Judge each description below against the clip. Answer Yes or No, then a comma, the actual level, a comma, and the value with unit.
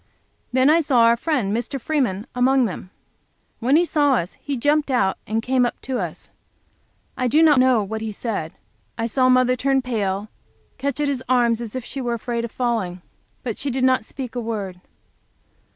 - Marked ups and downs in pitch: No, average, 3.1 semitones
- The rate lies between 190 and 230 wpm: Yes, average, 200 wpm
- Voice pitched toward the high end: Yes, high, 245 Hz